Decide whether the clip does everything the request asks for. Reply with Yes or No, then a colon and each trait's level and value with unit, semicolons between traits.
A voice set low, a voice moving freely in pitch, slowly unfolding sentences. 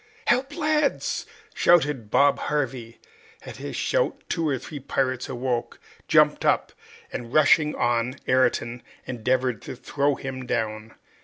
No: low, 130 Hz; average, 3.8 semitones; slow, 130 wpm